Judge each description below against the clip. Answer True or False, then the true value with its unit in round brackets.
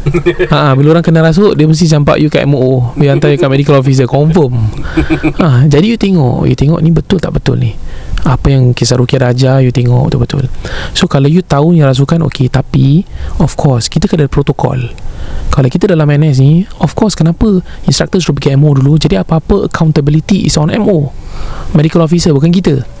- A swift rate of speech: True (195 wpm)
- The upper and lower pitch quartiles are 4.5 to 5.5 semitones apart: False (4.0 semitones)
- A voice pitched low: False (150 Hz)